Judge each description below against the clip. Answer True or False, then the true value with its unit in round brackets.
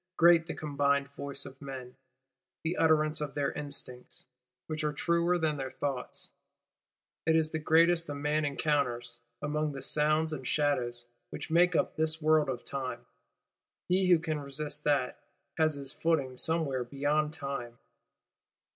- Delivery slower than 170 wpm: True (155 wpm)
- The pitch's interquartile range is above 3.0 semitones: False (2.5 semitones)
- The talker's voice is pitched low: False (150 Hz)